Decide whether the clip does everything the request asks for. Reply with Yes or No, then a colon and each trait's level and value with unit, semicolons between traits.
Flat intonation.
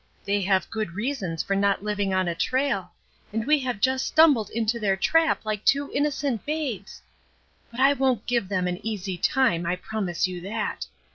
No: wide, 5.4 semitones